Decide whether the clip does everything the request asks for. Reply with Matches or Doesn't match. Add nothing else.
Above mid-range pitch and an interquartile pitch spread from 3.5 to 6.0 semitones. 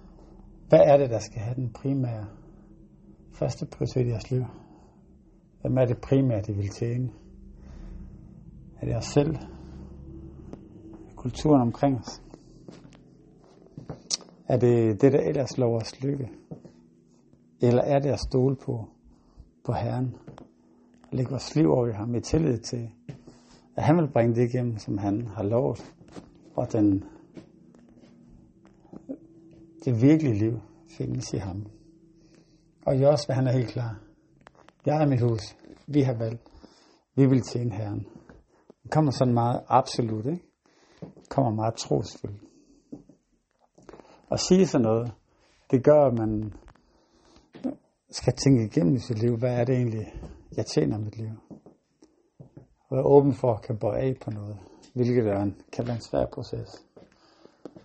Doesn't match